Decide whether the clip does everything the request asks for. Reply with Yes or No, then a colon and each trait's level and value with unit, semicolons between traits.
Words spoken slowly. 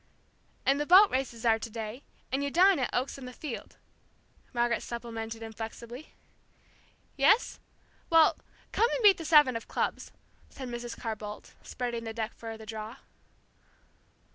No: average, 155 wpm